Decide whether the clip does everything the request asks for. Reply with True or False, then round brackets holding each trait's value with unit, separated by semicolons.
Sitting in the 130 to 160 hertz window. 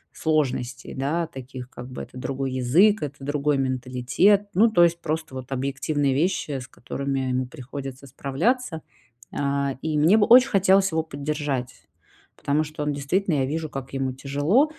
True (140 Hz)